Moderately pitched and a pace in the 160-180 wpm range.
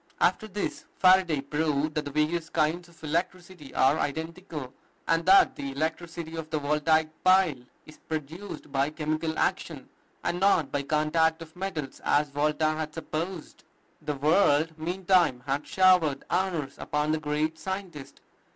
No: medium, 155 Hz; average, 145 wpm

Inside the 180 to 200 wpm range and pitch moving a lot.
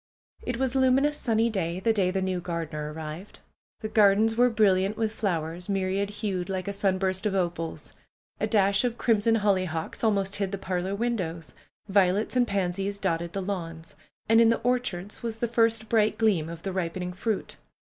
No: average, 190 wpm; average, 3.6 semitones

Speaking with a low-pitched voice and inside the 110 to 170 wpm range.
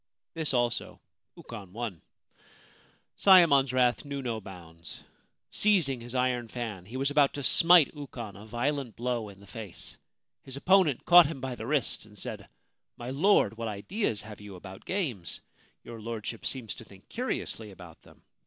Yes: low, 120 Hz; average, 165 wpm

